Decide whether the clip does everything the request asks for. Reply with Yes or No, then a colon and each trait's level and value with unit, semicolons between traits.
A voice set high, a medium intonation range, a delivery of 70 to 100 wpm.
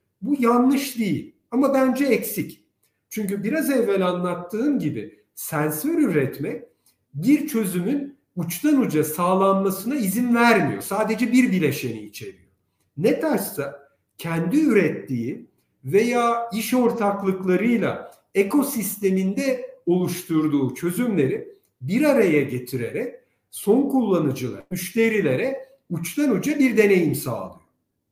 No: high, 210 Hz; wide, 7.1 semitones; slow, 95 wpm